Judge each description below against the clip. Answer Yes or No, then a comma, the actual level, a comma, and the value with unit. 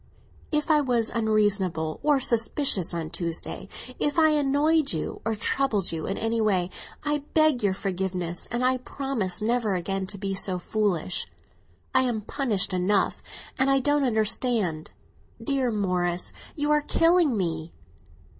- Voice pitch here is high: Yes, high, 220 Hz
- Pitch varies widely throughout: Yes, wide, 6.6 semitones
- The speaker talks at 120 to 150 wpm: Yes, average, 140 wpm